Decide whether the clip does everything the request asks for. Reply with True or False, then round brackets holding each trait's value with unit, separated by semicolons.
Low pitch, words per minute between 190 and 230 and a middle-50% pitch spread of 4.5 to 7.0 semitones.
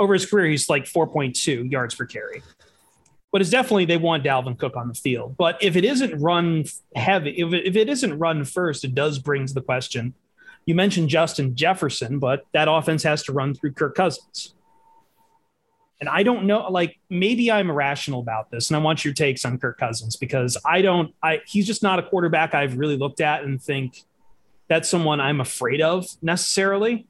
False (160 Hz; 200 wpm; 5.5 semitones)